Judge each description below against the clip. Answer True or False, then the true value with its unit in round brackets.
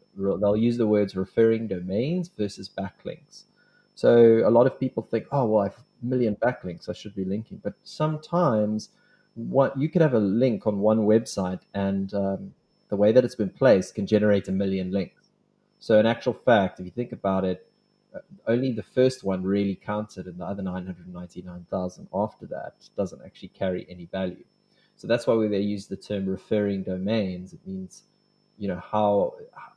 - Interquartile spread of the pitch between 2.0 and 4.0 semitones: True (3.7 semitones)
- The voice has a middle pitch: False (105 Hz)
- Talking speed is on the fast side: False (185 wpm)